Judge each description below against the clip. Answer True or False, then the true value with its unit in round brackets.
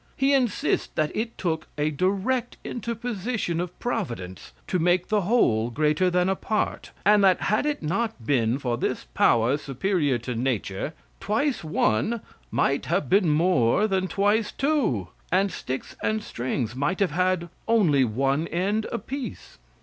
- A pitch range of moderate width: False (7.5 semitones)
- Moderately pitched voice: True (180 Hz)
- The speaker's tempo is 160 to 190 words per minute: False (150 wpm)